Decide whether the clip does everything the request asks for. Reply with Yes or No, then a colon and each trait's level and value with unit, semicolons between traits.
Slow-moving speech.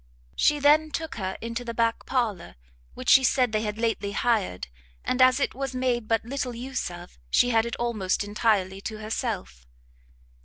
No: average, 180 wpm